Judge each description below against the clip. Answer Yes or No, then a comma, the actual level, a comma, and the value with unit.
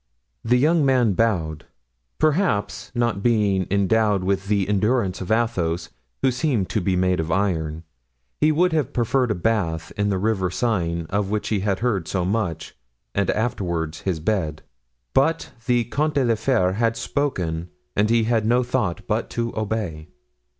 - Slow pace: No, average, 165 wpm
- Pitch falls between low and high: No, low, 105 Hz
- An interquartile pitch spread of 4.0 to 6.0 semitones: Yes, average, 4.5 semitones